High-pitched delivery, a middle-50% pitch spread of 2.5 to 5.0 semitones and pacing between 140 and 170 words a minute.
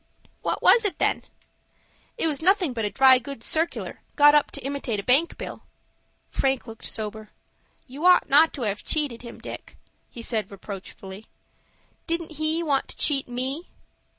No: very high, 270 Hz; wide, 5.5 semitones; average, 165 wpm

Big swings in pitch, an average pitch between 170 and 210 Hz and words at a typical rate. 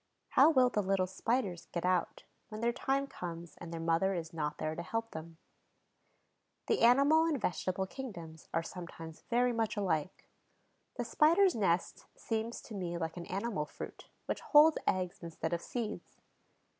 Yes: wide, 6.0 semitones; high, 190 Hz; average, 165 wpm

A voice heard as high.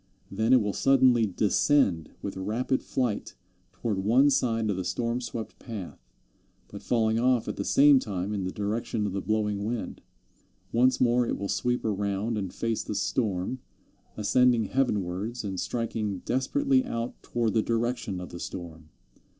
No: low, 110 Hz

